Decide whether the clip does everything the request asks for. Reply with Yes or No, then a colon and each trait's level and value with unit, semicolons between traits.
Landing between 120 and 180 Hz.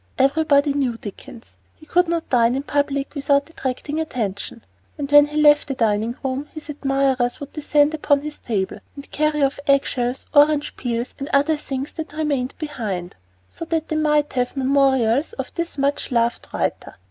No: very high, 280 Hz